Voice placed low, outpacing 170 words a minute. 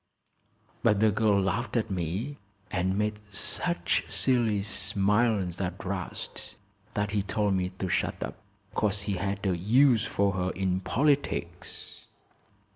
No: low, 100 Hz; slow, 135 wpm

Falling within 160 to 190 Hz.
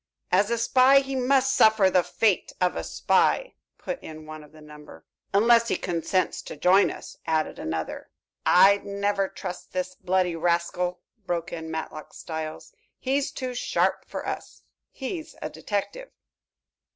Yes: medium, 185 Hz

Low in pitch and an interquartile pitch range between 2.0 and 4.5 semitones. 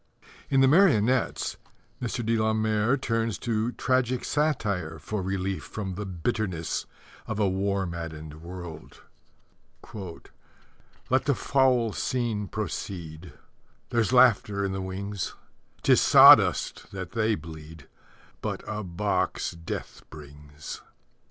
No: low, 100 Hz; average, 4.9 semitones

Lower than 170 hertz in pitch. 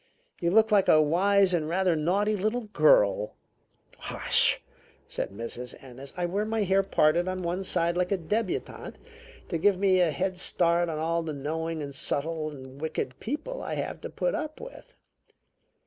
No: medium, 175 Hz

